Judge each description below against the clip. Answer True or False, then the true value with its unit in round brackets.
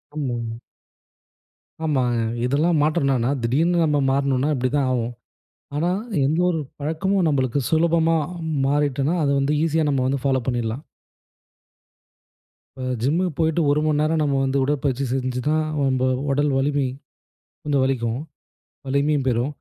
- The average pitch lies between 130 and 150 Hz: True (140 Hz)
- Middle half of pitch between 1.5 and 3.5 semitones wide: True (3.0 semitones)